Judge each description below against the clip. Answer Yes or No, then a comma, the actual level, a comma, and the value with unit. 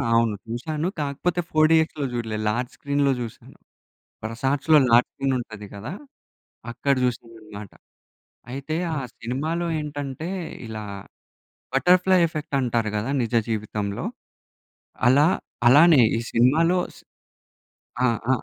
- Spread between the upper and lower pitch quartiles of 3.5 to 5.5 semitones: Yes, average, 5.2 semitones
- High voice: No, low, 135 Hz